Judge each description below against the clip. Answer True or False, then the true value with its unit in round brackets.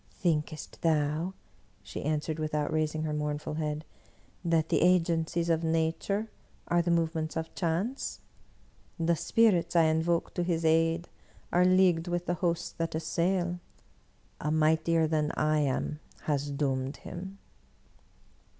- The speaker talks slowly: True (130 wpm)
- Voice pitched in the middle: True (165 Hz)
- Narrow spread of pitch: True (2.0 semitones)